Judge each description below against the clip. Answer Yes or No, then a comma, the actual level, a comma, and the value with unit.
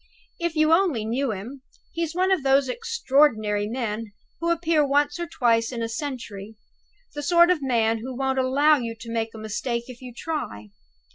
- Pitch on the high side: Yes, very high, 260 Hz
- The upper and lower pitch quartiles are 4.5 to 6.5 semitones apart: Yes, average, 5.2 semitones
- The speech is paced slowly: No, average, 185 wpm